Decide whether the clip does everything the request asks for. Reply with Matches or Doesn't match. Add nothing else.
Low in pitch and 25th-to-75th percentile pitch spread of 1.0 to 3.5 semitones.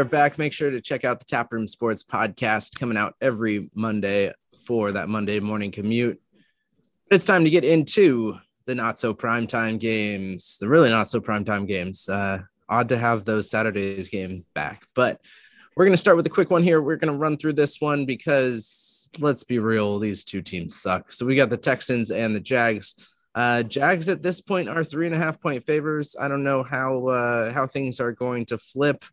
Doesn't match